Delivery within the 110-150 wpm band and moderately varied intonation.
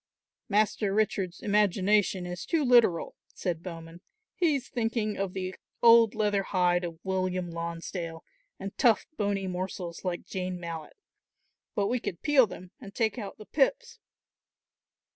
Yes: average, 140 wpm; average, 3.6 semitones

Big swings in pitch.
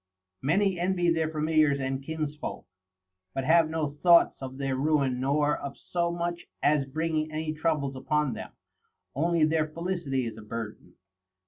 No: average, 3.3 semitones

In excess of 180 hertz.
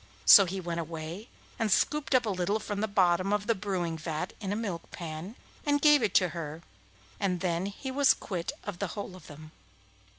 Yes: high, 190 Hz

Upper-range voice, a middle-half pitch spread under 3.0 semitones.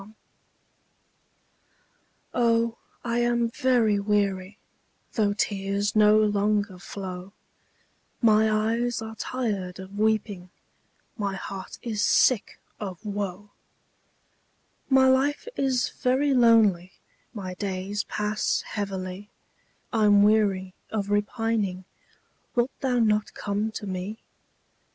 Yes: high, 210 Hz; narrow, 2.6 semitones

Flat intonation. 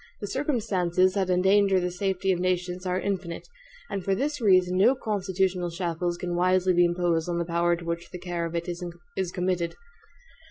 Yes: narrow, 1.7 semitones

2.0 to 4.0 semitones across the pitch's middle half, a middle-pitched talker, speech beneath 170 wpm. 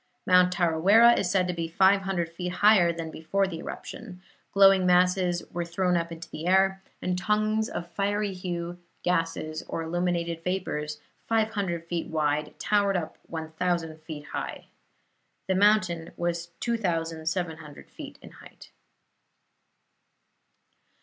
Yes: narrow, 2.6 semitones; medium, 175 Hz; slow, 135 wpm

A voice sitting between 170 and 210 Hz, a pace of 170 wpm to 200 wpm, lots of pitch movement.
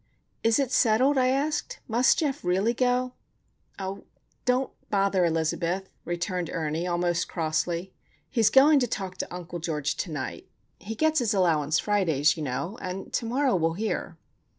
No: high, 190 Hz; average, 155 wpm; wide, 6.6 semitones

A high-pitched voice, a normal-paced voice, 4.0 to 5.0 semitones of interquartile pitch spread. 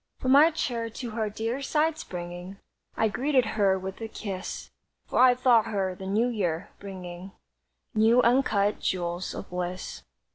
Yes: high, 215 Hz; average, 155 wpm; average, 4.7 semitones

